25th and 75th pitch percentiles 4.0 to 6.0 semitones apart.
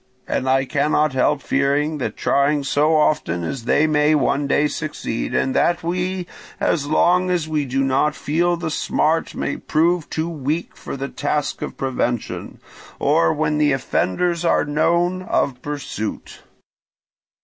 No: average, 2.9 semitones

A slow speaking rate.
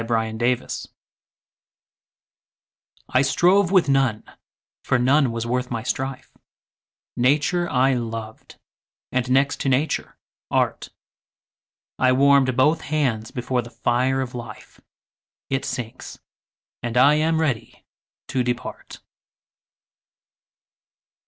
Yes: slow, 105 wpm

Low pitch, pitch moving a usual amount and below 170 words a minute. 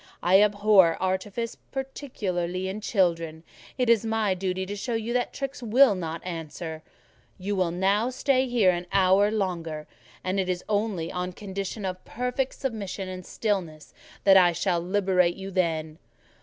No: high, 190 Hz; average, 3.3 semitones; average, 155 wpm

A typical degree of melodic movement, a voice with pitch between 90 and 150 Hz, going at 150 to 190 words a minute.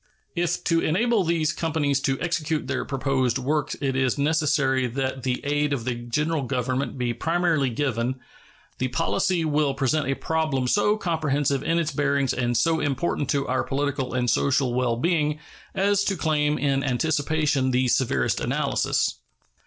Yes: average, 3.4 semitones; medium, 140 Hz; average, 160 wpm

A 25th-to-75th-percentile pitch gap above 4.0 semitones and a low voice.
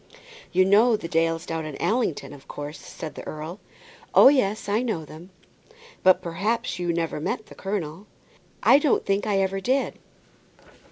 No: average, 4.7 semitones; medium, 185 Hz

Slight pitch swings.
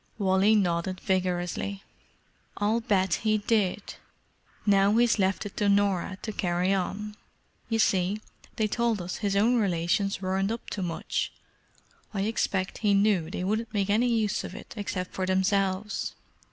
Yes: narrow, 2.2 semitones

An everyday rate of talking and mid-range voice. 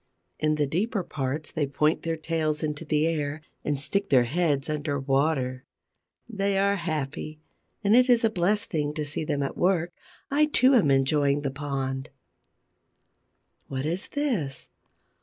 Yes: average, 160 wpm; medium, 155 Hz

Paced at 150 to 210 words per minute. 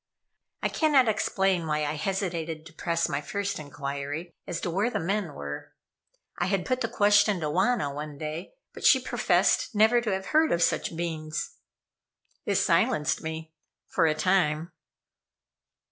Yes: average, 160 wpm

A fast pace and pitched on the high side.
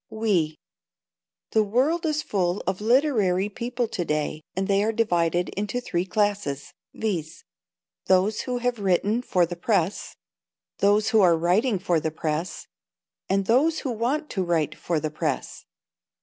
No: average, 150 wpm; high, 200 Hz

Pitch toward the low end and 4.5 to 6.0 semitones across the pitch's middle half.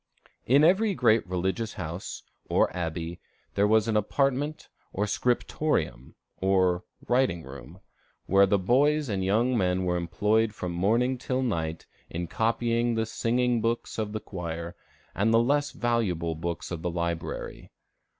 Yes: low, 105 Hz; wide, 5.5 semitones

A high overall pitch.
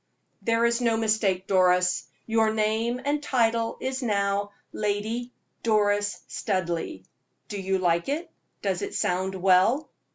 Yes: high, 215 Hz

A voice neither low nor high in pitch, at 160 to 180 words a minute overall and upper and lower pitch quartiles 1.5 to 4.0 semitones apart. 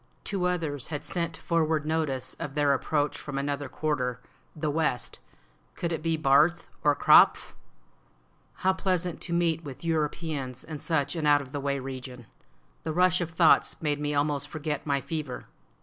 Yes: medium, 150 Hz; average, 165 wpm; narrow, 2.6 semitones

